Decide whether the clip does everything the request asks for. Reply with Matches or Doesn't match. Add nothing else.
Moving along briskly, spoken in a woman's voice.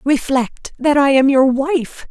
Doesn't match